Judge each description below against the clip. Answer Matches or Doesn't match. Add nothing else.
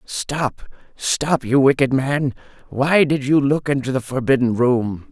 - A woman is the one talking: Doesn't match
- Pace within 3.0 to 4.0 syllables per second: Matches